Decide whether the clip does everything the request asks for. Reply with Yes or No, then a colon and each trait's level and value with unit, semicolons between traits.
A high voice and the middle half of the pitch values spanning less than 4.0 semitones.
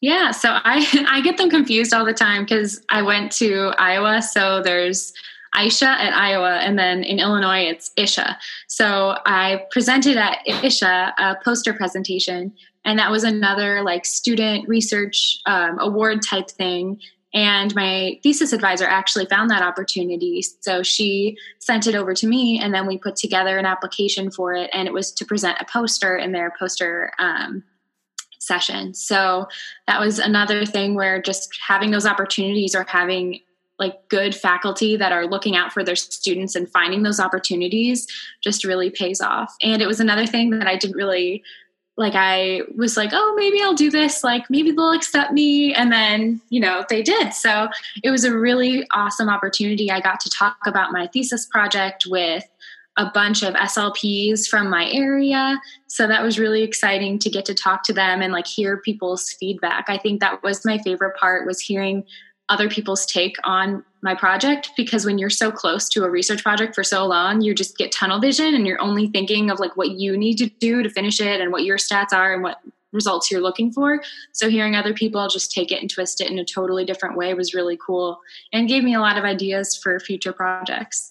Yes: high, 200 Hz; average, 2.8 semitones